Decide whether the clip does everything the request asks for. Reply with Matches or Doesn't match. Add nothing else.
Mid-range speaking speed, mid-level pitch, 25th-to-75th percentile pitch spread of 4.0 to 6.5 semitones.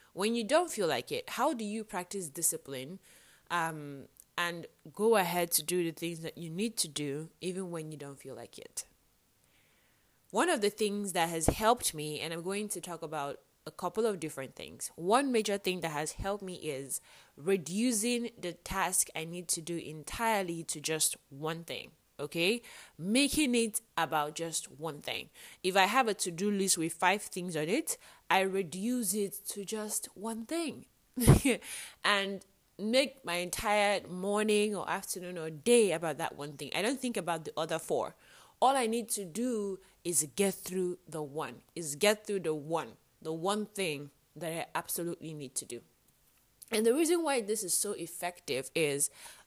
Matches